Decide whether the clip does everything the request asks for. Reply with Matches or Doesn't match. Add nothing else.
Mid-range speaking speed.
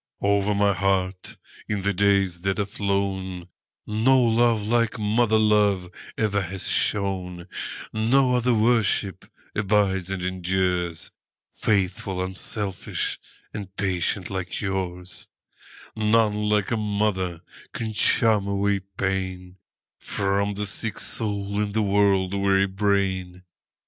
Doesn't match